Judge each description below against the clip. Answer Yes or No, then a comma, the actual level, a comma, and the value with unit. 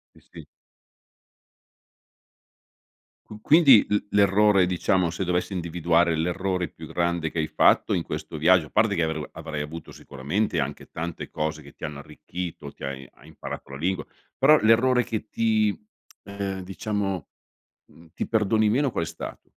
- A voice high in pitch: No, very low, 90 Hz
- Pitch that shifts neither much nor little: Yes, average, 4.6 semitones